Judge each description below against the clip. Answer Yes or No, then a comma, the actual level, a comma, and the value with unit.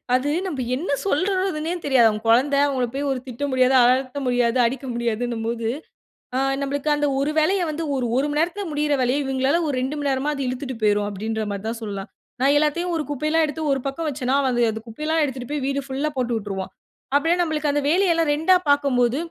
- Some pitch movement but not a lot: Yes, average, 3.6 semitones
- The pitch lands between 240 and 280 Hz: Yes, very high, 275 Hz